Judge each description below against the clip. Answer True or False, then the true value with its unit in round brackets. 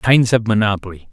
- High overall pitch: False (105 Hz)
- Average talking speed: True (160 wpm)